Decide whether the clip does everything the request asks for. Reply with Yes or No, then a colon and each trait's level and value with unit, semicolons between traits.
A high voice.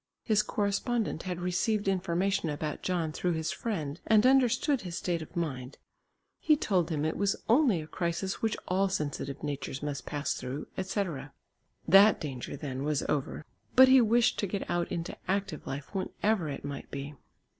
No: medium, 175 Hz